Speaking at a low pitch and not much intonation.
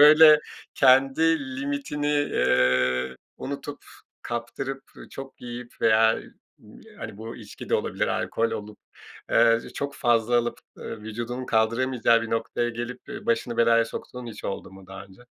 No: low, 120 Hz; average, 3.3 semitones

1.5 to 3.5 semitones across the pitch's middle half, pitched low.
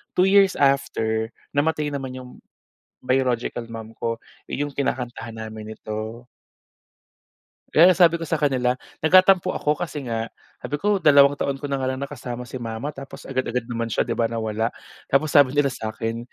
No: average, 4.1 semitones; low, 130 Hz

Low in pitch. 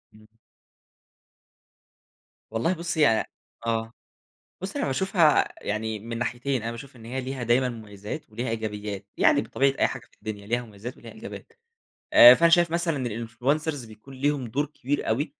Yes: low, 120 Hz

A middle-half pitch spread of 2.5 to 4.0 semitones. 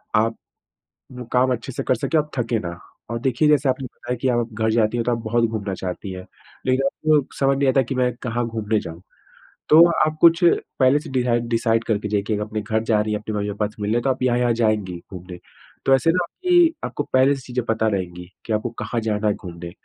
Yes: average, 3.6 semitones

